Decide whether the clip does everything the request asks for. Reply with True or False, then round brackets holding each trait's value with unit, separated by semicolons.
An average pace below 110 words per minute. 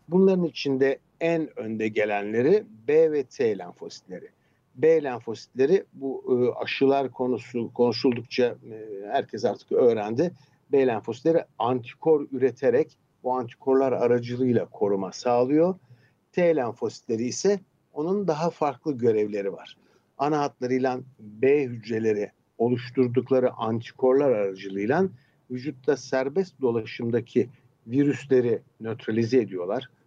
True (95 wpm)